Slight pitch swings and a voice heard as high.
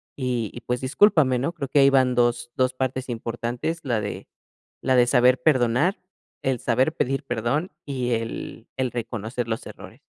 No: narrow, 2.1 semitones; low, 125 Hz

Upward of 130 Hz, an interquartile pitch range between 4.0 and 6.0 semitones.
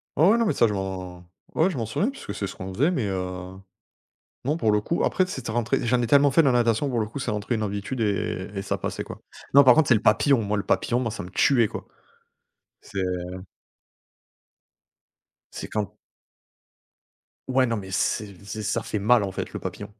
No: low, 110 Hz; average, 4.8 semitones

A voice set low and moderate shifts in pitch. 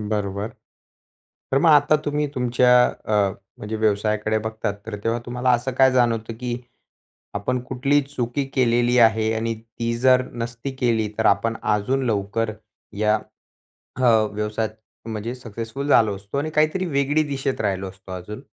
Yes: low, 115 Hz; average, 3.2 semitones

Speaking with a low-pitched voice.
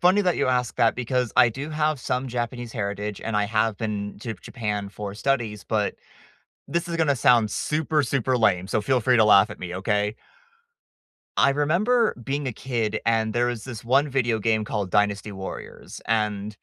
Yes: low, 115 Hz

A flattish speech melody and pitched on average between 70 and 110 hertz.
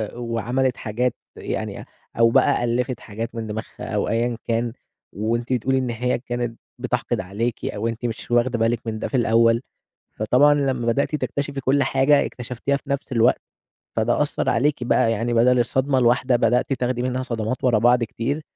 No: narrow, 2.0 semitones; low, 120 Hz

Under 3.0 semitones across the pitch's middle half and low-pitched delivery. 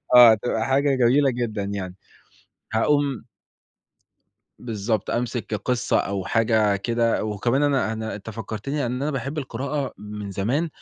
No: average, 4.1 semitones; low, 115 Hz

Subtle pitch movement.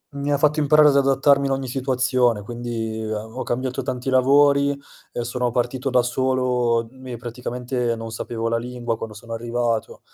Yes: narrow, 2.3 semitones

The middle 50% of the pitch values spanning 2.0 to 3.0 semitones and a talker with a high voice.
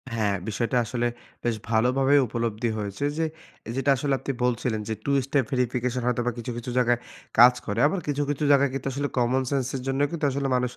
No: narrow, 2.6 semitones; low, 125 Hz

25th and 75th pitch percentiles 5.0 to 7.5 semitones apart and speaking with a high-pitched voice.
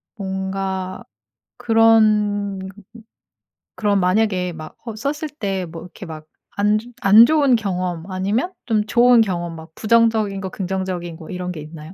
No: average, 3.5 semitones; high, 195 Hz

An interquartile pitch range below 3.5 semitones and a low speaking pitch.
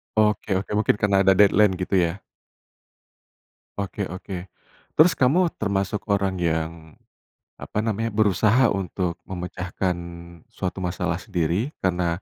Yes: average, 2.9 semitones; very low, 95 Hz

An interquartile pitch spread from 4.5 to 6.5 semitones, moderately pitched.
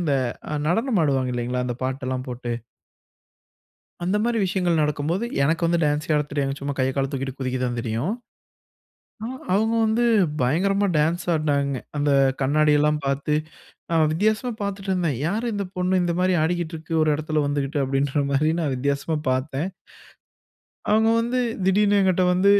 Yes: average, 5.2 semitones; medium, 155 Hz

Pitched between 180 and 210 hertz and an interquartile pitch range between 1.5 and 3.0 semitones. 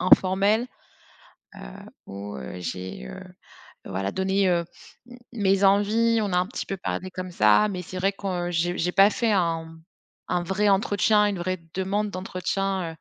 Yes: medium, 185 Hz; narrow, 2.6 semitones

